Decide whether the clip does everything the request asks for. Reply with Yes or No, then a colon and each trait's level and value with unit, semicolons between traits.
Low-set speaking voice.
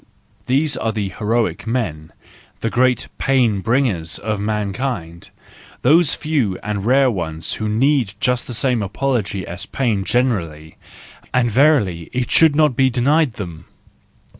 Yes: low, 115 Hz